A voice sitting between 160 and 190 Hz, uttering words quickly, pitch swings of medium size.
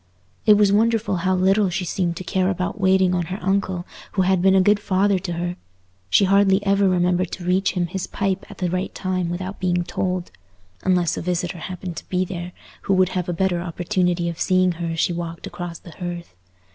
No: medium, 185 Hz; fast, 210 wpm; narrow, 1.5 semitones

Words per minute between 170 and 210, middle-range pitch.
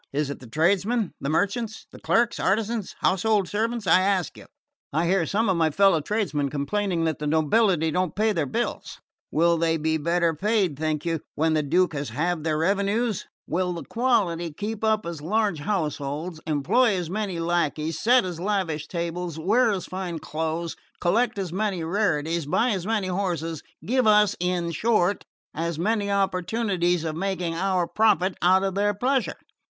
Yes: average, 175 wpm; medium, 180 Hz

